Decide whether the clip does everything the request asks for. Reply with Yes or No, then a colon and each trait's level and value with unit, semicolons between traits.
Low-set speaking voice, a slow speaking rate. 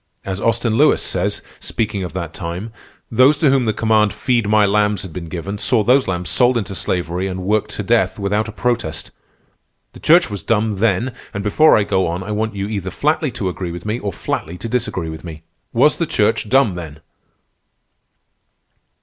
No: low, 105 Hz; average, 195 wpm